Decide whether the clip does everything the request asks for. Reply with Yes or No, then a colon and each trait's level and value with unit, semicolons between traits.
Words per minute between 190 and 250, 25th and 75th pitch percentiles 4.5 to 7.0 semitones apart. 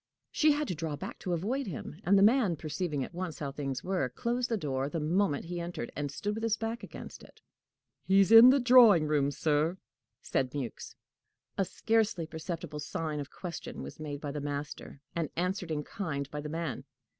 Yes: average, 200 wpm; wide, 5.4 semitones